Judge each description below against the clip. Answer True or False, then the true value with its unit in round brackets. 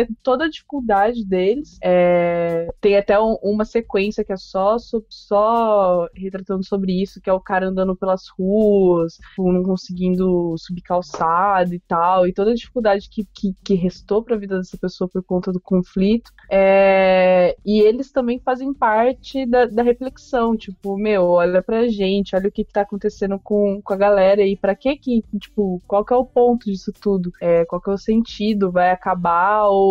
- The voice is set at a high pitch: True (200 Hz)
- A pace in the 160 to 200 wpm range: True (180 wpm)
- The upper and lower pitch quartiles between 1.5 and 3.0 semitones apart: True (2.7 semitones)